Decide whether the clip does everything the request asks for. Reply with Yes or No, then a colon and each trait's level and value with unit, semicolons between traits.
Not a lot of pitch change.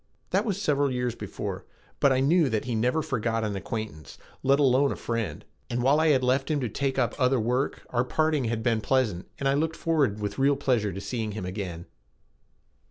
No: average, 4.1 semitones